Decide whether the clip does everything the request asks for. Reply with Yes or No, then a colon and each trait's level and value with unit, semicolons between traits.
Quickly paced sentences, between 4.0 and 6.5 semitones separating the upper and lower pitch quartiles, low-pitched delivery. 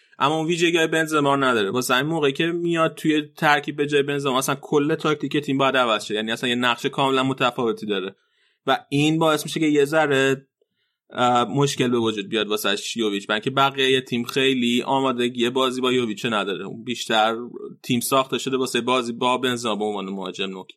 No: fast, 185 wpm; average, 3.2 semitones; low, 130 Hz